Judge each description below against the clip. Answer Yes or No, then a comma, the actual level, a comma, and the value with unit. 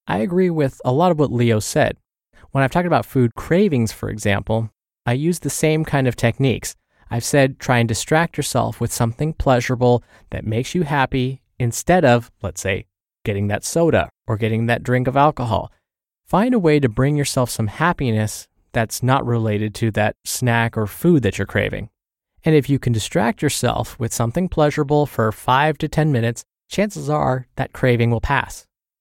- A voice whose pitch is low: Yes, low, 125 Hz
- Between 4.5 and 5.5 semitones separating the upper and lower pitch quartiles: Yes, average, 4.8 semitones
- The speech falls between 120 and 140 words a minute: No, average, 185 wpm